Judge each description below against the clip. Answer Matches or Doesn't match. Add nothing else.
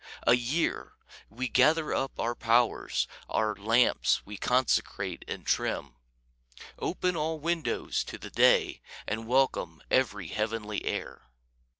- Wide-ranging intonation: Doesn't match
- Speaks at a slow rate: Matches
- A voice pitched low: Matches